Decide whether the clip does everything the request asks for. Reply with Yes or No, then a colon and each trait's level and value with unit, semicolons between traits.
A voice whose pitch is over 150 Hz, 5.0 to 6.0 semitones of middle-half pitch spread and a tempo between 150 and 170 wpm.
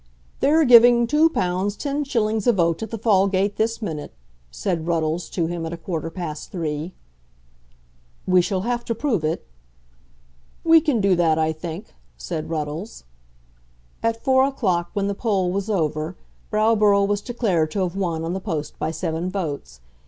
Yes: high, 190 Hz; average, 5.3 semitones; average, 160 wpm